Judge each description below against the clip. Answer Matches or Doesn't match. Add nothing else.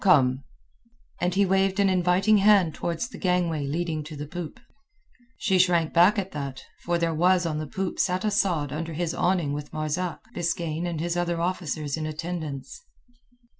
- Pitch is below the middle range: Doesn't match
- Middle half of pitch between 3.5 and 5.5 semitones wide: Doesn't match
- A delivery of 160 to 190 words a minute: Matches